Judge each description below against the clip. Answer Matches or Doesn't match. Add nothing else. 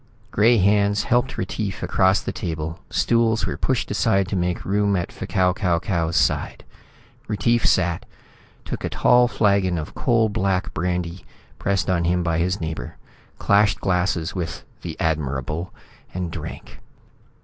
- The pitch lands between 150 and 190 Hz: Doesn't match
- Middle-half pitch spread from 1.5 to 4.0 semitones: Matches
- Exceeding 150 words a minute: Doesn't match